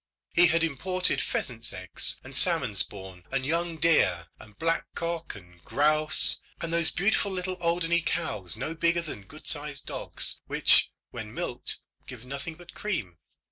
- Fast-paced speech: No, average, 155 wpm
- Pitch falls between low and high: Yes, medium, 160 Hz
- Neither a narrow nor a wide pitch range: No, wide, 7.5 semitones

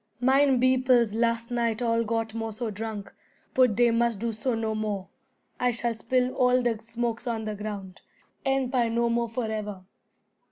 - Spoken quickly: No, average, 170 wpm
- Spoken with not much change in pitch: Yes, narrow, 2.0 semitones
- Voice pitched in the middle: No, high, 230 Hz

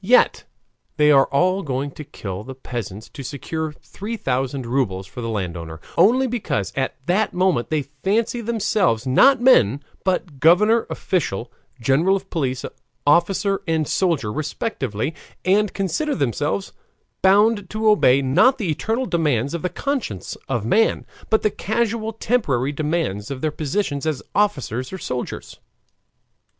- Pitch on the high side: No, medium, 155 Hz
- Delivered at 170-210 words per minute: No, average, 145 wpm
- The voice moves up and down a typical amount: No, wide, 7.9 semitones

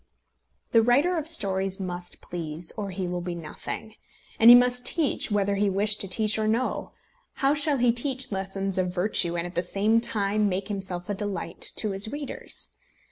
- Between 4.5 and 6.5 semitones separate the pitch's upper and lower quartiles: No, average, 4.1 semitones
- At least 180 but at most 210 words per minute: Yes, average, 190 wpm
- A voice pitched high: Yes, high, 205 Hz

